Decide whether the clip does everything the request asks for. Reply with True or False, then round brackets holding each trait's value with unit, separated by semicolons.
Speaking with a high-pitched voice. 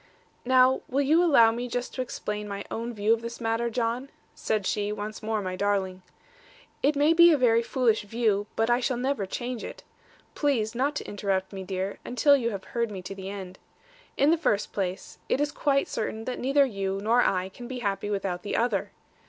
True (225 Hz)